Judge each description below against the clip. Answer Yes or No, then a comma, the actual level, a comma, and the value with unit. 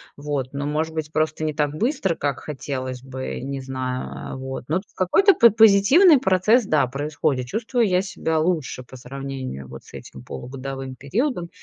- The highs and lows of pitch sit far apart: Yes, wide, 5.9 semitones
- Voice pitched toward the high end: No, medium, 145 Hz